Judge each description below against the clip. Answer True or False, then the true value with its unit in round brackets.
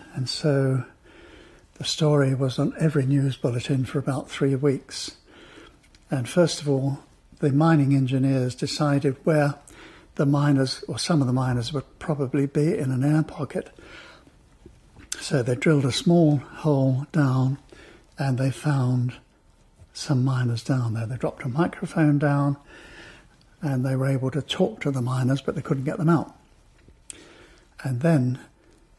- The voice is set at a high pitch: False (140 Hz)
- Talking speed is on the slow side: False (150 wpm)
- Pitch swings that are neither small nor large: False (2.2 semitones)